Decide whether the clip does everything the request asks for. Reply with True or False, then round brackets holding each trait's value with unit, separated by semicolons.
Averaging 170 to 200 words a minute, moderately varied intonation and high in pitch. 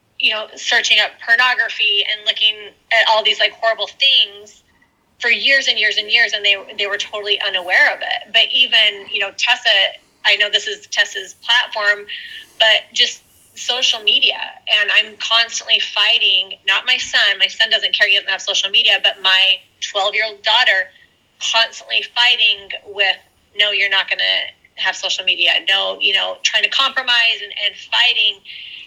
True (175 wpm; 3.3 semitones; 215 Hz)